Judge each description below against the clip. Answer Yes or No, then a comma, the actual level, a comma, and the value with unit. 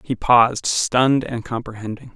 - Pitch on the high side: No, low, 120 Hz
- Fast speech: No, average, 140 wpm